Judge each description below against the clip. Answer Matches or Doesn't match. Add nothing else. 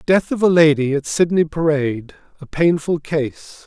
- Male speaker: Matches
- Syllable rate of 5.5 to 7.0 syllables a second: Doesn't match